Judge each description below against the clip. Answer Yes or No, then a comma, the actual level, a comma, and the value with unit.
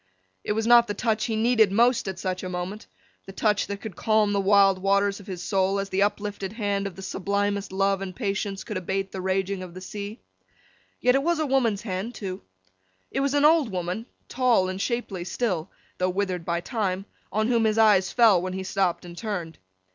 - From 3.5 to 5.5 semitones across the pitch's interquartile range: No, average, 2.8 semitones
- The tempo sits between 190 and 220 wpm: Yes, fast, 205 wpm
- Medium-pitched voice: No, high, 200 Hz